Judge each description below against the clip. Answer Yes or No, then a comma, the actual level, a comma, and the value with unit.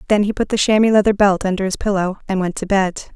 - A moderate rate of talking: No, fast, 265 wpm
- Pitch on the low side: No, high, 200 Hz